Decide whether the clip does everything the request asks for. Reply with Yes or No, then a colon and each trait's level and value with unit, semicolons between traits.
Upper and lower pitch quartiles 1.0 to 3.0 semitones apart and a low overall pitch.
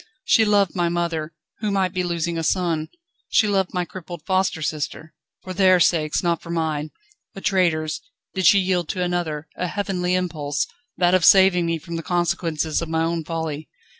No: narrow, 2.4 semitones; medium, 175 Hz